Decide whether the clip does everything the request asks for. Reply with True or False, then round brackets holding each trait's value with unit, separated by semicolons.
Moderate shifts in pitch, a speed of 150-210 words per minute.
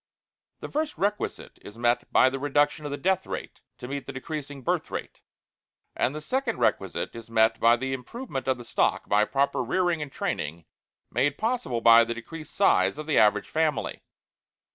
True (4.7 semitones; 185 wpm)